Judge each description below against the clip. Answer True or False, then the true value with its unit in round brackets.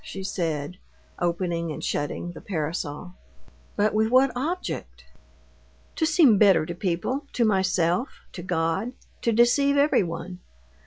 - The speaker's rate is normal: False (125 wpm)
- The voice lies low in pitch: False (185 Hz)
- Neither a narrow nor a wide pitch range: False (6.1 semitones)